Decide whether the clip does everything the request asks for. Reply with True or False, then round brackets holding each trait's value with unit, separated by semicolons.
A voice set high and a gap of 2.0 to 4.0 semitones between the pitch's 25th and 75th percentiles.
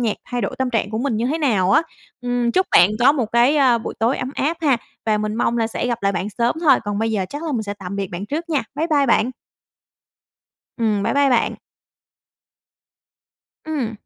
False (235 Hz; 4.6 semitones)